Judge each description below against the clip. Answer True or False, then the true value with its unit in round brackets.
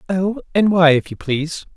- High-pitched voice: False (170 Hz)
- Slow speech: False (205 wpm)